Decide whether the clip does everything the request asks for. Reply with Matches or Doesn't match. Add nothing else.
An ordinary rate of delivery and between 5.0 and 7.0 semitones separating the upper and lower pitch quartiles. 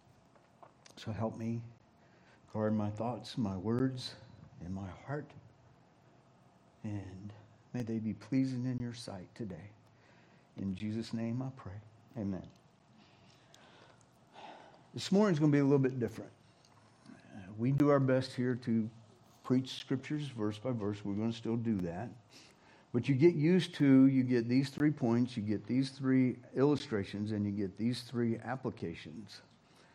Doesn't match